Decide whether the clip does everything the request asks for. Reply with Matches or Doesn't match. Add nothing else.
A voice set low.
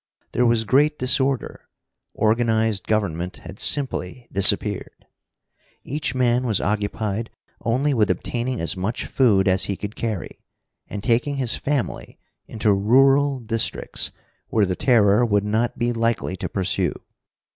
Matches